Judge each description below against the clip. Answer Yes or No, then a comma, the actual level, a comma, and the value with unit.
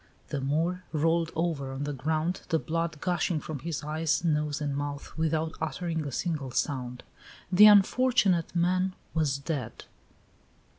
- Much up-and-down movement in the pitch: No, average, 2.8 semitones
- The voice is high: No, medium, 160 Hz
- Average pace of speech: Yes, average, 145 wpm